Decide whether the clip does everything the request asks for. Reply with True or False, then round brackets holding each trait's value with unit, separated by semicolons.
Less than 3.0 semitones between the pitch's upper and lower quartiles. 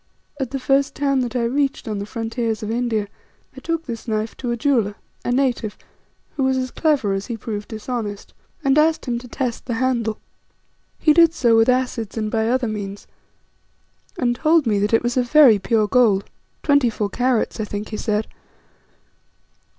False (3.3 semitones)